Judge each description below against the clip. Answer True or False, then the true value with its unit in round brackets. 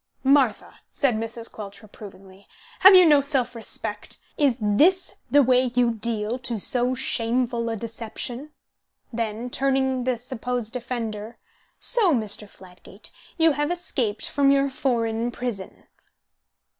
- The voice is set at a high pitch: True (240 Hz)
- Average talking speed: False (130 wpm)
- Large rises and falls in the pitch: False (3.2 semitones)